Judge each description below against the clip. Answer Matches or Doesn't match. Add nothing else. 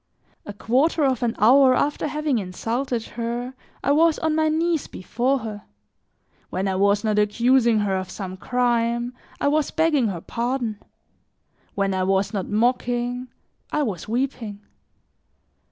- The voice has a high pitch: Matches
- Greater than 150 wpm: Doesn't match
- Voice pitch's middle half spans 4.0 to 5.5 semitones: Matches